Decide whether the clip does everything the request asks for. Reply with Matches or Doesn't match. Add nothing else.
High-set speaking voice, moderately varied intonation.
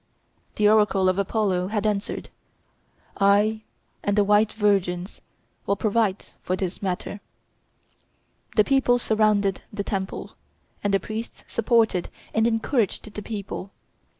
Doesn't match